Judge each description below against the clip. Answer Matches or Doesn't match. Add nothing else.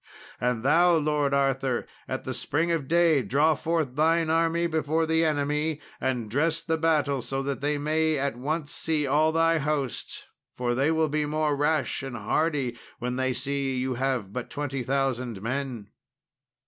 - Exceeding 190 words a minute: Doesn't match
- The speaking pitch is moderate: Matches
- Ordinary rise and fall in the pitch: Matches